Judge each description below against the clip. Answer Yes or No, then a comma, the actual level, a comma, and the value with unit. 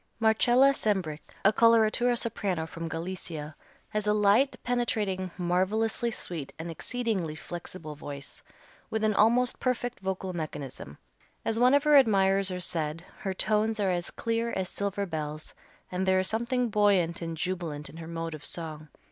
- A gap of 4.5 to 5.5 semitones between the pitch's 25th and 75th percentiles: Yes, average, 5.1 semitones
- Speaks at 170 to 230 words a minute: No, average, 155 wpm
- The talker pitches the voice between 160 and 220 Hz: Yes, high, 190 Hz